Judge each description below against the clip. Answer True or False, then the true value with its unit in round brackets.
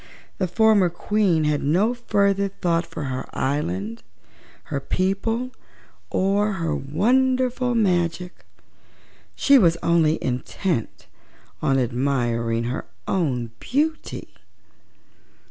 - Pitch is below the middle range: False (175 Hz)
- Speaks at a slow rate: True (95 wpm)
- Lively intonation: True (7.4 semitones)